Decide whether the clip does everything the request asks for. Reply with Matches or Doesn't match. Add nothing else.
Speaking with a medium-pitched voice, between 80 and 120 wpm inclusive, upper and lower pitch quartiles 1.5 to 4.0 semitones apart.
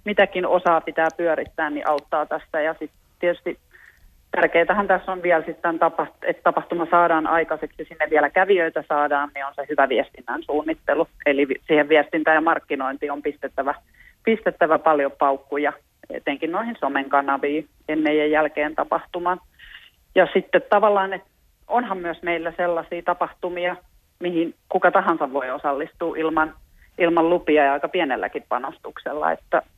Doesn't match